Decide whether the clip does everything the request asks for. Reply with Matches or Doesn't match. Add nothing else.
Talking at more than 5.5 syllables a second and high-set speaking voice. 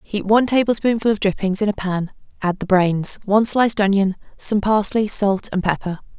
Doesn't match